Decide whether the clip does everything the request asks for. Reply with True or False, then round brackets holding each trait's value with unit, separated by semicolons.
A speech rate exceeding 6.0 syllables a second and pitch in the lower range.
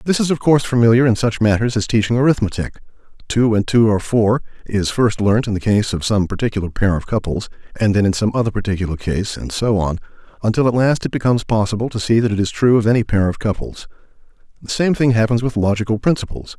True (6.4 syllables/s; 110 Hz)